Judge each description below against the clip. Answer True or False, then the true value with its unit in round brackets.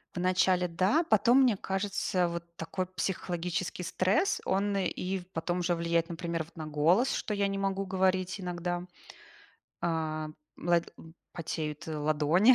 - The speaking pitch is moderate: True (180 Hz)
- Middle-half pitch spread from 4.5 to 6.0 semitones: False (2.4 semitones)